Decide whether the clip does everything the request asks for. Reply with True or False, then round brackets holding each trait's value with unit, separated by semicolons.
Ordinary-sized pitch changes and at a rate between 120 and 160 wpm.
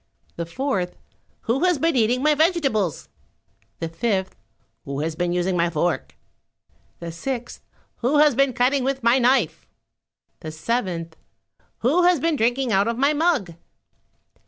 False (7.7 semitones; 145 wpm)